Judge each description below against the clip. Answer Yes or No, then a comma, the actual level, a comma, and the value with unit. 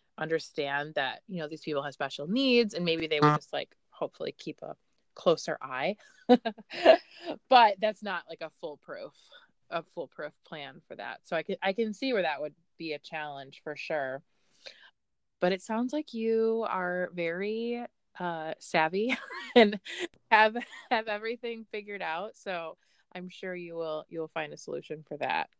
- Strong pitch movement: Yes, wide, 6.1 semitones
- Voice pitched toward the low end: No, medium, 185 Hz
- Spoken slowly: No, average, 165 wpm